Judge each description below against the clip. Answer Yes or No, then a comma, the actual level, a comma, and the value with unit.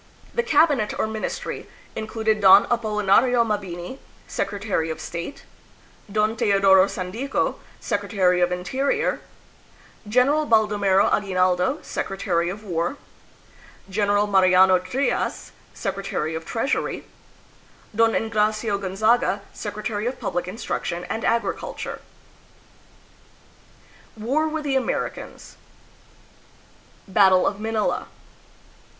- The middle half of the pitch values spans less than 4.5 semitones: Yes, average, 3.3 semitones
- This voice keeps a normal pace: No, slow, 95 wpm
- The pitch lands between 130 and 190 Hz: No, high, 210 Hz